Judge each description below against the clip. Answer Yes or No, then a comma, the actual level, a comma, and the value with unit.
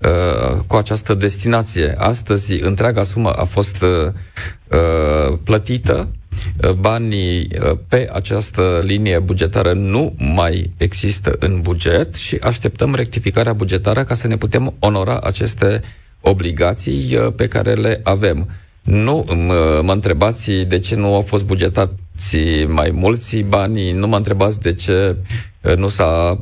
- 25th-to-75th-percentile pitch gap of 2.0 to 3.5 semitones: Yes, average, 3.2 semitones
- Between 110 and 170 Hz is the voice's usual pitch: No, very low, 95 Hz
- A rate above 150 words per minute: No, average, 135 wpm